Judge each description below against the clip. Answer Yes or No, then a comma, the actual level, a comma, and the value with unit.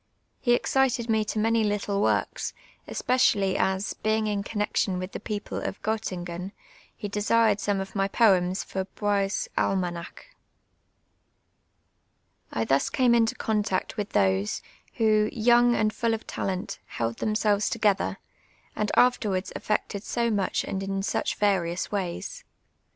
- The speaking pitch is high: Yes, high, 205 Hz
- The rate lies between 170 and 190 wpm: No, slow, 135 wpm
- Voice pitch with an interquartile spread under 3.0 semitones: Yes, narrow, 2.6 semitones